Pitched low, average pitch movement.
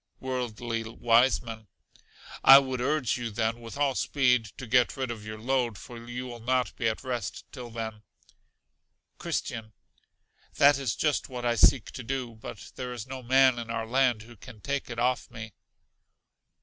No: low, 120 Hz; narrow, 2.2 semitones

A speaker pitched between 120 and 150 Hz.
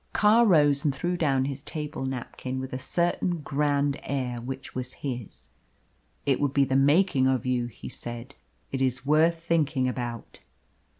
Yes: low, 135 Hz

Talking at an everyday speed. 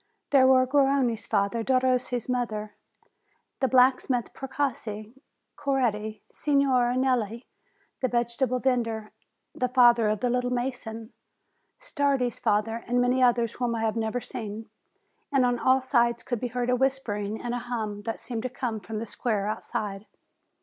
Yes: average, 150 wpm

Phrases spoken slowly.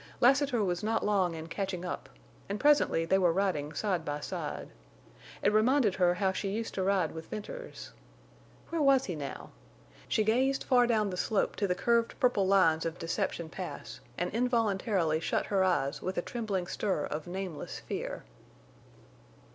No: average, 170 wpm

